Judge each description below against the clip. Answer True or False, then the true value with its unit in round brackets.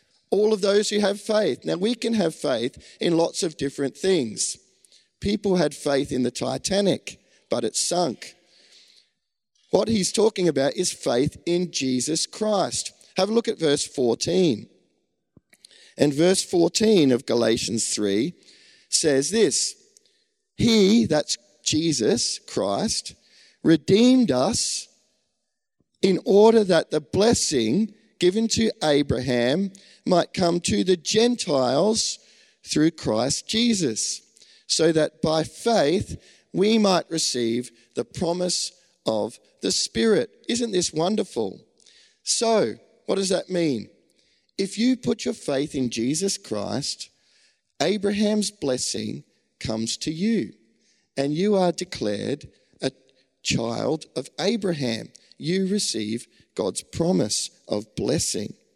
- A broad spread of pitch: True (7.0 semitones)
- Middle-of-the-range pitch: True (180 Hz)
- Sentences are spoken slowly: True (120 wpm)